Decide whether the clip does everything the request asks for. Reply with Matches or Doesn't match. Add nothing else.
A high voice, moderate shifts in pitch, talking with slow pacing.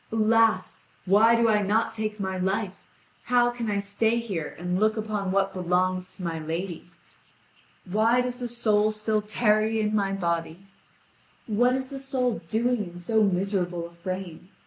Doesn't match